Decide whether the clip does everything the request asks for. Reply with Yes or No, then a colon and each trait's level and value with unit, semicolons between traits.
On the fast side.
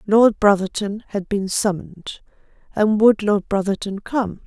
No: slow, 135 wpm